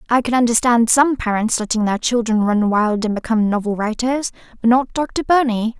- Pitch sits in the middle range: No, high, 230 Hz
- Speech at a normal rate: Yes, average, 185 wpm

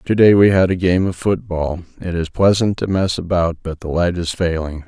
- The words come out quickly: Yes, fast, 220 wpm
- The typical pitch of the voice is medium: No, very low, 90 Hz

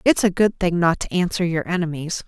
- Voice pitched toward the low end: No, medium, 175 Hz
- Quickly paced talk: Yes, fast, 235 wpm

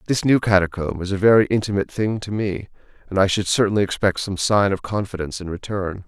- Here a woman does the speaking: No, male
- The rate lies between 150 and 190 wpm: No, fast, 205 wpm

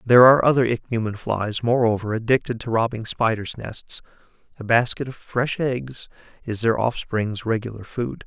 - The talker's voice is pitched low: Yes, low, 115 Hz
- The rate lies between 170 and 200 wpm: No, average, 150 wpm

